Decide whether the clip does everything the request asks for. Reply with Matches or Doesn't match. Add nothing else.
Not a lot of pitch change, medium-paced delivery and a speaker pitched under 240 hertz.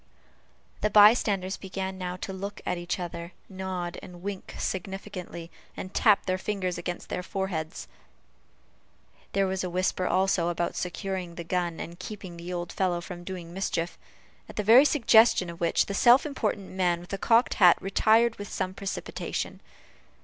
Matches